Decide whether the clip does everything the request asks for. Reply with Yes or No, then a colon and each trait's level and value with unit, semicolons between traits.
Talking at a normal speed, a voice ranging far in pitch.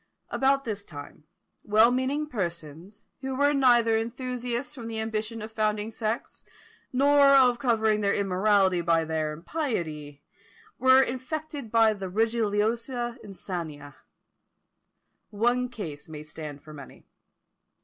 No: slow, 120 wpm; wide, 5.7 semitones